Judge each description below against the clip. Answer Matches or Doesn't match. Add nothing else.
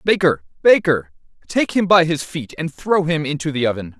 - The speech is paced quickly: Doesn't match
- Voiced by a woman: Doesn't match